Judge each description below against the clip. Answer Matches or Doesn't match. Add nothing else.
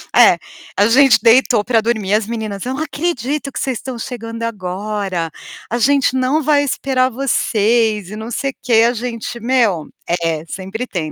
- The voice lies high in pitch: Matches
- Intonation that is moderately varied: Matches